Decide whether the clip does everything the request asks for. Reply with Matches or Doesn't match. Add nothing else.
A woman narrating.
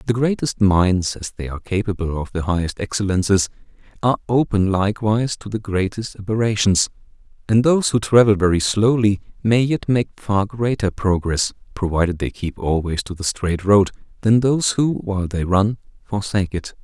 Doesn't match